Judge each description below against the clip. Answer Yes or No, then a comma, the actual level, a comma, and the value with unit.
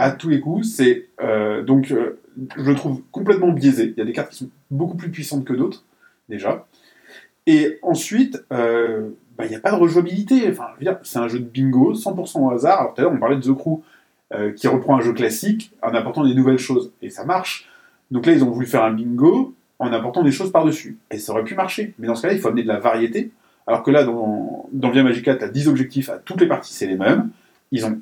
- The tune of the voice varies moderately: No, wide, 6.5 semitones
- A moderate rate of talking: No, fast, 250 wpm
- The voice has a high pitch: No, low, 135 Hz